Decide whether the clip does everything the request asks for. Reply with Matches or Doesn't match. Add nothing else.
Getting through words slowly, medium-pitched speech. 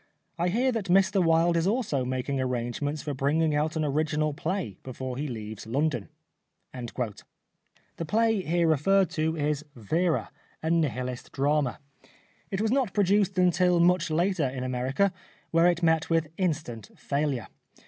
Doesn't match